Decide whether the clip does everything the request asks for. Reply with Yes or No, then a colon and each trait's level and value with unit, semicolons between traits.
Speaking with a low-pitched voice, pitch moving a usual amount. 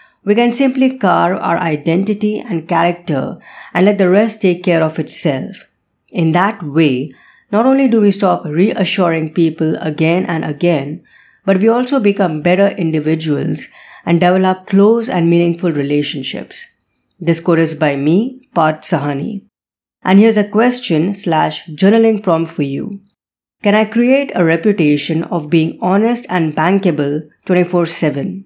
No: medium, 175 Hz; average, 4.3 semitones